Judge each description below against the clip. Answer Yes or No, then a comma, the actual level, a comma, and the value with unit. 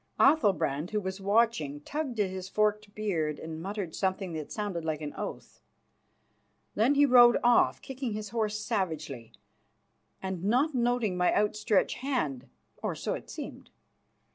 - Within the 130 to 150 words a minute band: Yes, average, 145 wpm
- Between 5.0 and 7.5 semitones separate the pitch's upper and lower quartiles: Yes, wide, 5.6 semitones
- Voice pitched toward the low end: No, high, 205 Hz